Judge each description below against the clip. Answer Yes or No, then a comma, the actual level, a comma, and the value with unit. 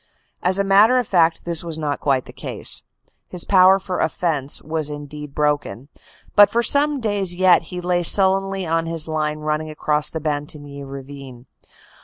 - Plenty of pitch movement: No, average, 4.2 semitones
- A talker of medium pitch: Yes, medium, 160 Hz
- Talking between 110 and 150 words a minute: No, average, 170 wpm